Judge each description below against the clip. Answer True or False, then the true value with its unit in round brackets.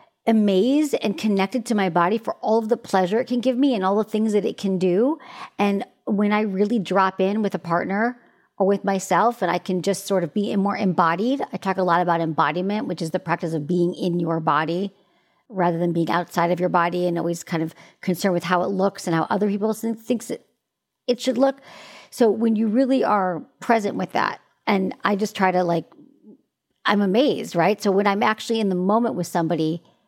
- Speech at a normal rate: False (215 wpm)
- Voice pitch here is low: False (195 Hz)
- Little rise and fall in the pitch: False (3.8 semitones)